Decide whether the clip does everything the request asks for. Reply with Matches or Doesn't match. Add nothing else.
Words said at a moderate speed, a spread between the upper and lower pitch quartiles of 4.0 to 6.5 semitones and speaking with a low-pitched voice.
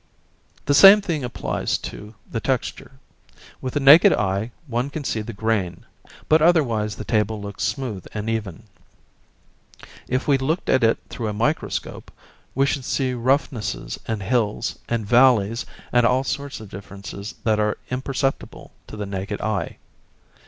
Matches